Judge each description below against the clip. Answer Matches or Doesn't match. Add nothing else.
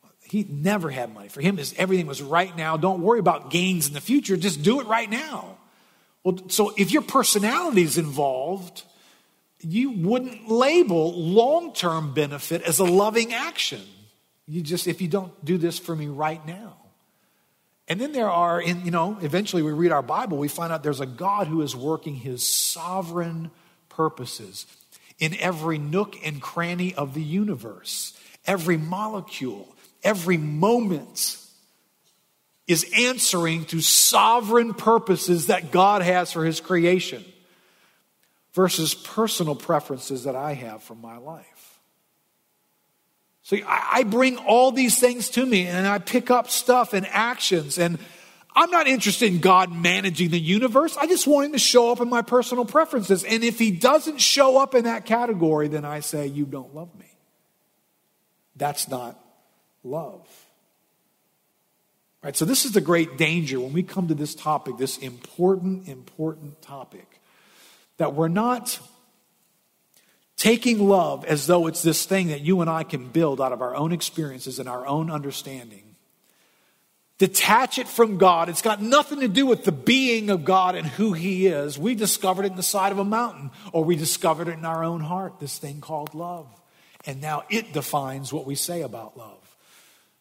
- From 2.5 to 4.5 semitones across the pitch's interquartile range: Doesn't match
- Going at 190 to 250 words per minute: Doesn't match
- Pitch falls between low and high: Matches